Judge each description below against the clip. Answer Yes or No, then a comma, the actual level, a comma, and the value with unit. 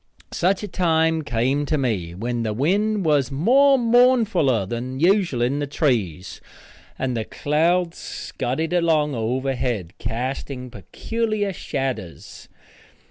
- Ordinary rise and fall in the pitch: No, wide, 6.7 semitones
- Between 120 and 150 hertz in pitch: Yes, medium, 140 Hz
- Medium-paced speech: No, slow, 120 wpm